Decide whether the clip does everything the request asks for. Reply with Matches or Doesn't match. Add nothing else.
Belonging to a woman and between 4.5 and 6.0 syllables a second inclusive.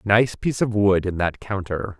Doesn't match